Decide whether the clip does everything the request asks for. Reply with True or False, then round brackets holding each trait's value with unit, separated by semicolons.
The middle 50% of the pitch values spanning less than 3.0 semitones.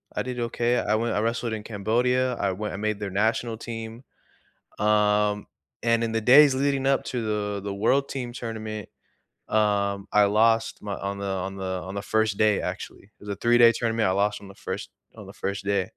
True (2.5 semitones)